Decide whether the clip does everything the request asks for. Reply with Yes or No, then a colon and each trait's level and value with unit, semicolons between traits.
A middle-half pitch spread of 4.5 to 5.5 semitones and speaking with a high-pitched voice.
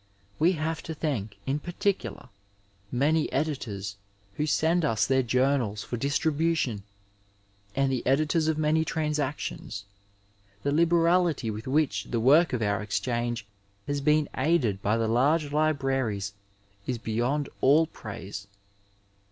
No: average, 5.0 semitones; medium, 140 Hz